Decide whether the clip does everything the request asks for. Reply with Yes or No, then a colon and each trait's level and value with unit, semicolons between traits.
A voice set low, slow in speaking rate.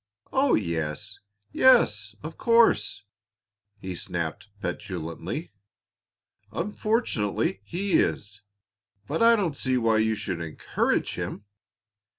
Yes: low, 110 Hz; slow, 100 wpm